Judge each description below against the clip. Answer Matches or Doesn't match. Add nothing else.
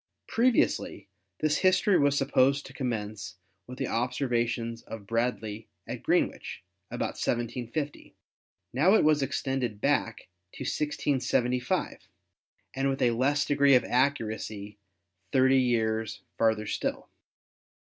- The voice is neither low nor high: Doesn't match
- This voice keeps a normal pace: Doesn't match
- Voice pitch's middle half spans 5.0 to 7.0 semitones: Doesn't match